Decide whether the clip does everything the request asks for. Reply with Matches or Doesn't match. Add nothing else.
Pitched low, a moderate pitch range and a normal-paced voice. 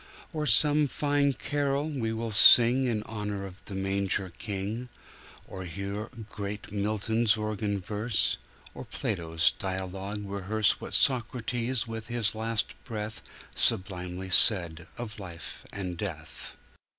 Doesn't match